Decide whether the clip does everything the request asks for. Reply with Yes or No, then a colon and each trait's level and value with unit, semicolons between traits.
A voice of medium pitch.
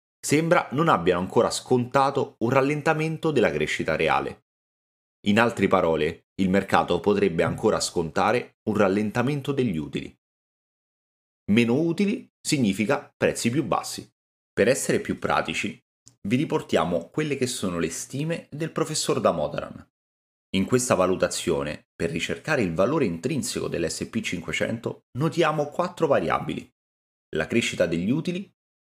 No: low, 125 Hz